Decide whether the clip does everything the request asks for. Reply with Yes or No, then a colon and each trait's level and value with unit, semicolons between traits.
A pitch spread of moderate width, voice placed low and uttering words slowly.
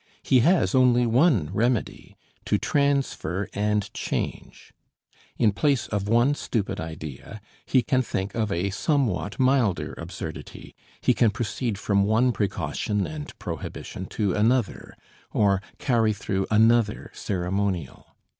Yes: average, 4.2 semitones; low, 110 Hz; slow, 125 wpm